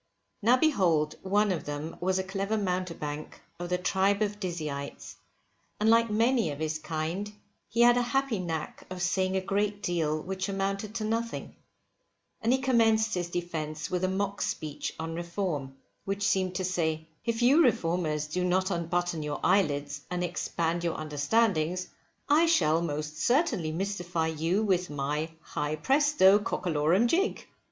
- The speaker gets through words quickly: No, average, 160 wpm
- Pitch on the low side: No, medium, 180 Hz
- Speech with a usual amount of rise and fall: Yes, average, 4.6 semitones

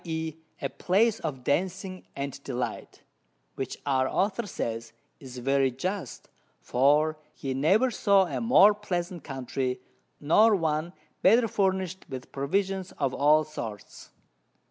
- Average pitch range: No, wide, 6.0 semitones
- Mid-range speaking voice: Yes, medium, 160 Hz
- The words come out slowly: Yes, slow, 125 wpm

